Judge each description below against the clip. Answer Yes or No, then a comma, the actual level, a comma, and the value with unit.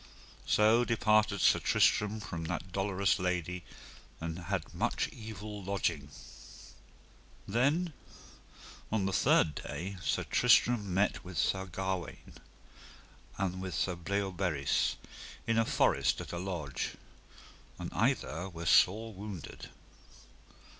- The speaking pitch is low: Yes, very low, 95 Hz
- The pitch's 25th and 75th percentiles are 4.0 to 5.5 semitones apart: No, average, 3.3 semitones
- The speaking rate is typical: No, slow, 115 wpm